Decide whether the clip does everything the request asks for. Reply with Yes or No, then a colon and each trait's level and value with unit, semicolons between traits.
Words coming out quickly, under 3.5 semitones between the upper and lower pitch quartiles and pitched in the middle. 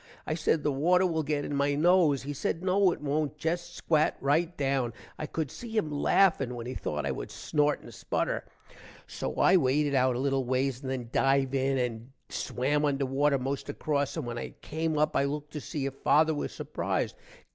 Yes: fast, 210 wpm; narrow, 2.6 semitones; medium, 145 Hz